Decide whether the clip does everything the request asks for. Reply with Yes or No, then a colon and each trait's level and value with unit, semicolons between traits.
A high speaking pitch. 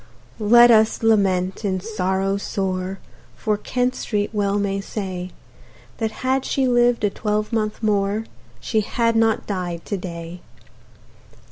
Yes: high, 205 Hz